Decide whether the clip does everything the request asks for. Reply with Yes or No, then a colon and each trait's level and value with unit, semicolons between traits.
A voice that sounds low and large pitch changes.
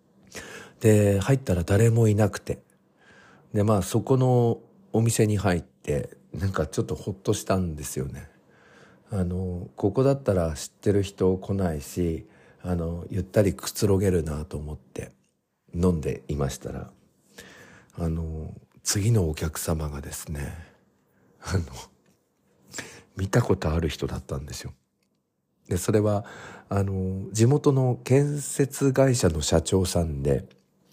No: very low, 95 Hz; average, 4.7 semitones